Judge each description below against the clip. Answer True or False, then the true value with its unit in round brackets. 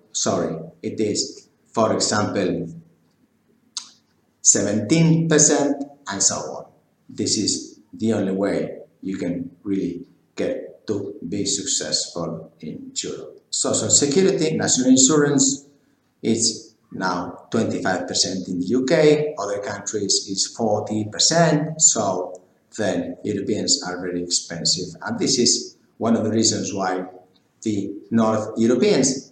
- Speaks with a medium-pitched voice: False (110 Hz)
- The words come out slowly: True (115 wpm)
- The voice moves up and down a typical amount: False (7.8 semitones)